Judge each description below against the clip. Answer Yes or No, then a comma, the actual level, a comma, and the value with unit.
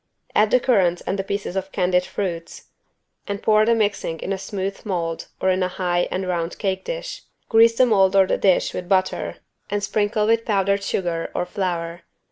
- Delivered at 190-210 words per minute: Yes, average, 195 wpm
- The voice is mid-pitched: No, high, 195 Hz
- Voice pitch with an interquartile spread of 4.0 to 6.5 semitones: No, narrow, 2.6 semitones